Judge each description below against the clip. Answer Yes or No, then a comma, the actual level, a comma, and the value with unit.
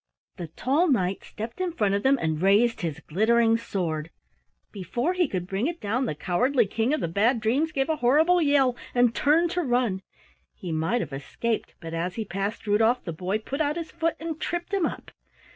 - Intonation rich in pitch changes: Yes, wide, 7.1 semitones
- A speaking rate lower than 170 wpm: No, fast, 205 wpm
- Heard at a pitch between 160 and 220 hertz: No, high, 230 Hz